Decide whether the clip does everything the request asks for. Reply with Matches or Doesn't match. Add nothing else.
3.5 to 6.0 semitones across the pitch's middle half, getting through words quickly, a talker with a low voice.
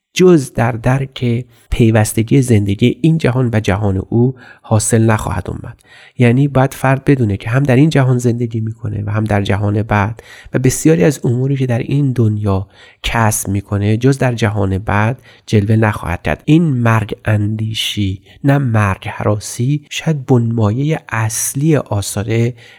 Doesn't match